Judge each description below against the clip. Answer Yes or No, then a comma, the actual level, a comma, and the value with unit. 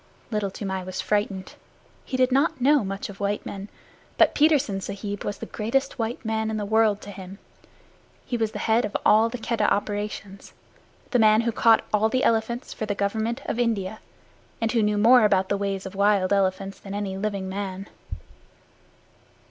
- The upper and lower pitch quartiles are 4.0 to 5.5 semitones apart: No, narrow, 2.4 semitones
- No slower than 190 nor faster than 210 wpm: No, average, 180 wpm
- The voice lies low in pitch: No, high, 210 Hz